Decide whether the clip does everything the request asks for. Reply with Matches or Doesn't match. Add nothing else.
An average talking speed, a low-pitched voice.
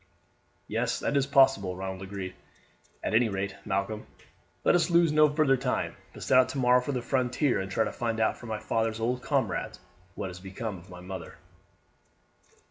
Matches